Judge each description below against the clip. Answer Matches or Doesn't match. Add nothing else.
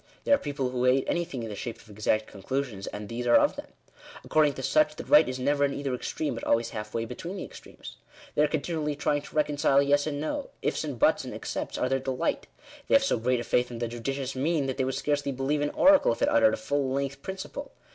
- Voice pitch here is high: Doesn't match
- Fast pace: Matches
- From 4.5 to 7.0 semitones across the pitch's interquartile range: Doesn't match